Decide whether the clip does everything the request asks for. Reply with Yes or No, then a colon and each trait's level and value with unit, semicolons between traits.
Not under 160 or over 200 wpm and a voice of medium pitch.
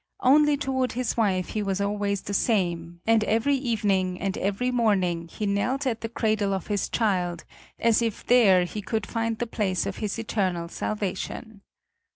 No: average, 175 wpm; high, 210 Hz